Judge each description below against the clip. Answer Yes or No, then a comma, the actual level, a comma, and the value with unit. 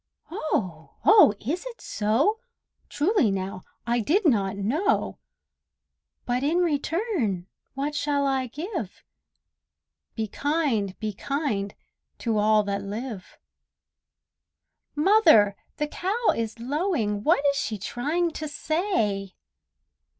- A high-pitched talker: Yes, very high, 265 Hz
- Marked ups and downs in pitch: Yes, wide, 7.6 semitones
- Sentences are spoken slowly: Yes, slow, 110 wpm